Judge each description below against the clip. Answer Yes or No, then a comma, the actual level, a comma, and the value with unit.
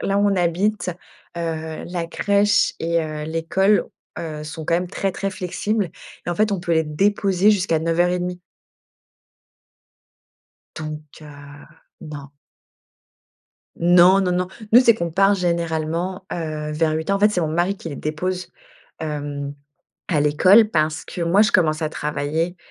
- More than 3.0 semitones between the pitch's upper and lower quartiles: Yes, average, 3.4 semitones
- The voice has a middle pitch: Yes, medium, 170 Hz